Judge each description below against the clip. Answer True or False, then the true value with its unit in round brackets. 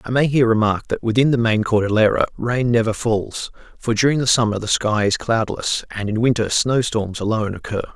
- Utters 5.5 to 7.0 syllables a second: True (5.6 syllables/s)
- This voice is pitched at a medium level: False (115 Hz)